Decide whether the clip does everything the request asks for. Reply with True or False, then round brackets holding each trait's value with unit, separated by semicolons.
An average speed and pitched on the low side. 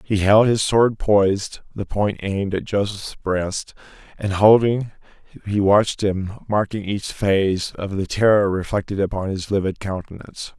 True (155 wpm; 100 Hz)